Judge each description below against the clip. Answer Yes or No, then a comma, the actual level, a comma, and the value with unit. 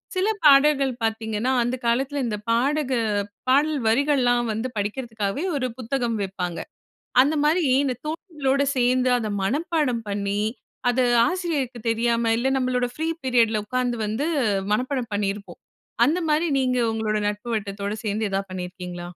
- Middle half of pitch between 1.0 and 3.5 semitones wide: No, average, 4.4 semitones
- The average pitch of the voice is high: Yes, high, 245 Hz